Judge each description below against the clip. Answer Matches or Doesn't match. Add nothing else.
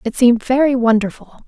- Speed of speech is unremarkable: Matches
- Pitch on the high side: Matches